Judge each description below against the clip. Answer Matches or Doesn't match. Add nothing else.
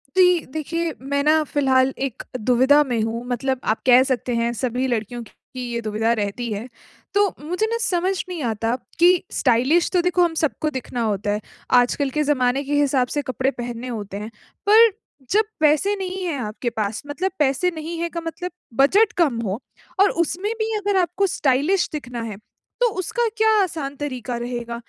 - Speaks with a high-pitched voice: Matches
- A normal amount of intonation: Doesn't match